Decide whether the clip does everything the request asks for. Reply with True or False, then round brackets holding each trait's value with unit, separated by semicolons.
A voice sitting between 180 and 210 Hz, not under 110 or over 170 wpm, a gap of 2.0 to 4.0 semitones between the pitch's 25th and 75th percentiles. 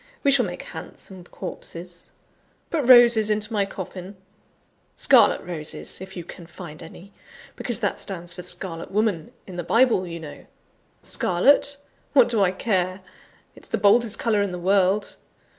True (190 Hz; 155 wpm; 3.7 semitones)